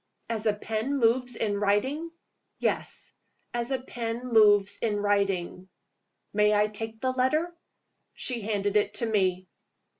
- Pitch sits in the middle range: No, high, 220 Hz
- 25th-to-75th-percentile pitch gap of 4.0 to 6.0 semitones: No, average, 3.1 semitones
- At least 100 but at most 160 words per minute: Yes, average, 140 wpm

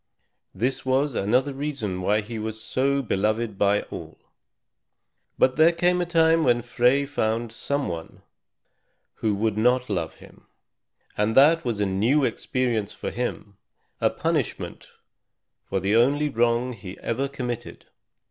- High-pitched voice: No, low, 120 Hz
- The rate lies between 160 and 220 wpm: No, average, 140 wpm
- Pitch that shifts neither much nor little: Yes, average, 4.5 semitones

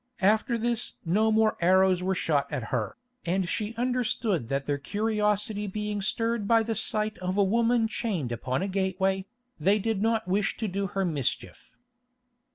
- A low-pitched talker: No, high, 200 Hz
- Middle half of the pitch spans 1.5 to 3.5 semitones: Yes, average, 3.1 semitones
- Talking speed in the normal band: Yes, average, 165 wpm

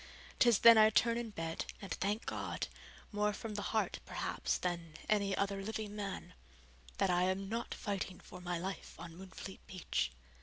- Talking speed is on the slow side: No, average, 175 wpm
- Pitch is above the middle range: Yes, high, 195 Hz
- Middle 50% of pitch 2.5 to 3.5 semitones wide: Yes, average, 2.8 semitones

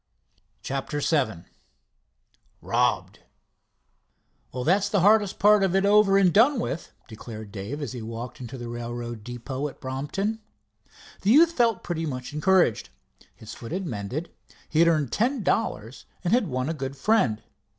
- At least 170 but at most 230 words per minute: No, average, 155 wpm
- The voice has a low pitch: No, medium, 150 Hz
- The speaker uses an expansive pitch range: Yes, wide, 8.5 semitones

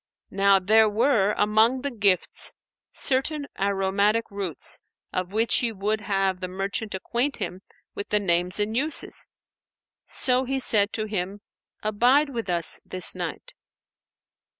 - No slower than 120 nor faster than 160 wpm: Yes, slow, 135 wpm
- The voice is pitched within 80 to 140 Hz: No, high, 210 Hz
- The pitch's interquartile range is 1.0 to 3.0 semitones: No, average, 3.5 semitones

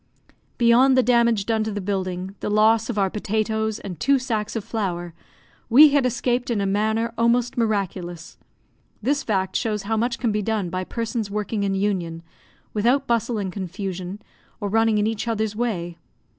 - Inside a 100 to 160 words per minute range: No, average, 175 wpm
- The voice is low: No, high, 215 Hz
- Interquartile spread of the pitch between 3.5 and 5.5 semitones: No, average, 3.0 semitones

